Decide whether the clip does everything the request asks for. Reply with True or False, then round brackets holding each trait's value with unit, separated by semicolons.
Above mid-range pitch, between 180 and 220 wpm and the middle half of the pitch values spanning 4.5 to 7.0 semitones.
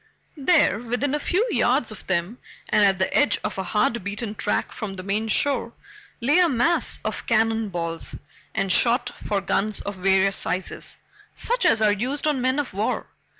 True (220 Hz; 185 wpm; 4.8 semitones)